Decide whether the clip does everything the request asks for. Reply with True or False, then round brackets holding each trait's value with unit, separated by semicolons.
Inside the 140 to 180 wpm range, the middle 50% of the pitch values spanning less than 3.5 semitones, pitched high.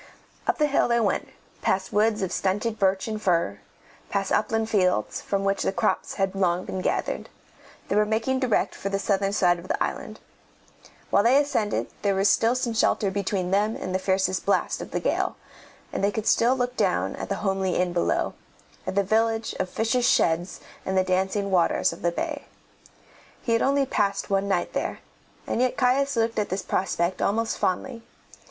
False (190 wpm; 3.1 semitones; 200 Hz)